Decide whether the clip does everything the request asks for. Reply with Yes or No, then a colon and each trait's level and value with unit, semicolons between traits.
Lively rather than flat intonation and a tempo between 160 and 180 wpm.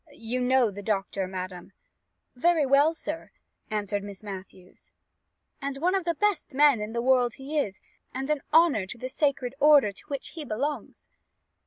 Yes: wide, 6.3 semitones; average, 175 wpm